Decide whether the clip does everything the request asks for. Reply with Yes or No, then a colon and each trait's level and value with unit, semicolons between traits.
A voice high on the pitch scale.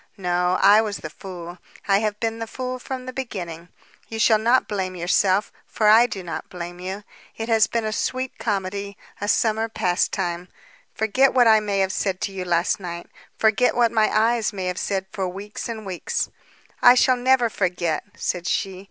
Yes: high, 205 Hz